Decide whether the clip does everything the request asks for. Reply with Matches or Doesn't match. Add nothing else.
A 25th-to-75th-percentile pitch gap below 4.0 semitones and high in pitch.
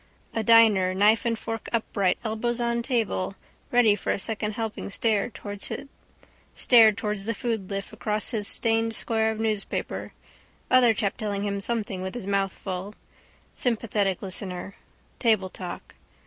Matches